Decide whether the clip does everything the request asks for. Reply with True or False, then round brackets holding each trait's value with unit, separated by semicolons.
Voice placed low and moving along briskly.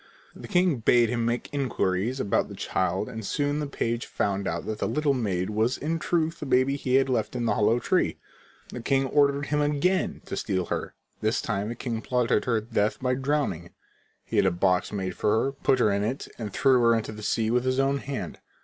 True (120 Hz; 220 wpm)